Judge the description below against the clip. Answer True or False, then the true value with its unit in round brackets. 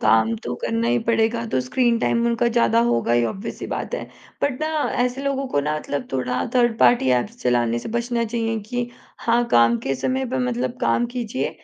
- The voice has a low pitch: False (225 Hz)